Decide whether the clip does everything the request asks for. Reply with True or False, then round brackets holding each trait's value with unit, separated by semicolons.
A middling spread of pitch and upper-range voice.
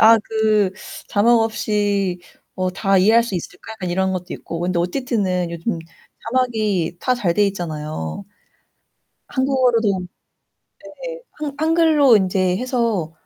True (4.6 semitones; 205 Hz)